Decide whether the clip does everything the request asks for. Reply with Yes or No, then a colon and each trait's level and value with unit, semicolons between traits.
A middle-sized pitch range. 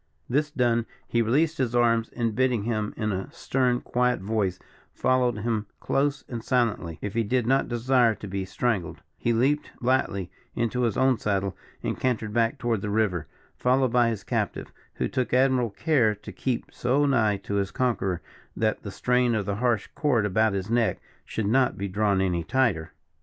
Yes: average, 3.5 semitones